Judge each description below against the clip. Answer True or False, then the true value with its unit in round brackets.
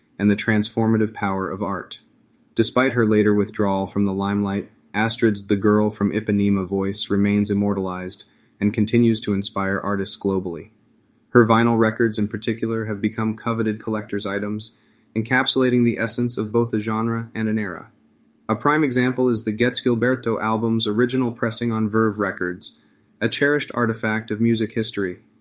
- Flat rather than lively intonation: True (2.1 semitones)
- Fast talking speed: False (155 wpm)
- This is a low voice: True (110 Hz)